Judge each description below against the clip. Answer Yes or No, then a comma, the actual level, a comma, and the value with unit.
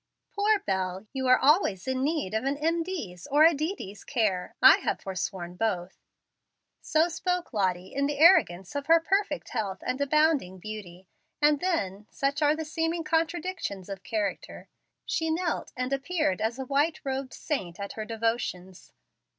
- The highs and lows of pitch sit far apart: Yes, wide, 8.5 semitones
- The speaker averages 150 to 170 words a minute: Yes, average, 165 wpm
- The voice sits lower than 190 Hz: No, very high, 270 Hz